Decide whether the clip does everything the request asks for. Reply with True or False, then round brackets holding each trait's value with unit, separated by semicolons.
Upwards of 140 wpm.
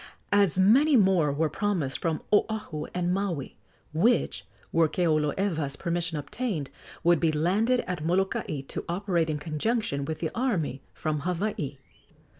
False (135 wpm)